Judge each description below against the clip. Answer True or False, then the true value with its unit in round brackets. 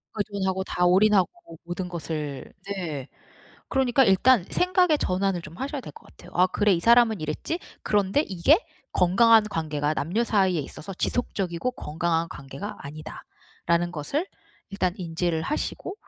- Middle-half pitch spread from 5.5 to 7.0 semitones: False (5.1 semitones)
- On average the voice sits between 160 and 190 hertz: True (185 Hz)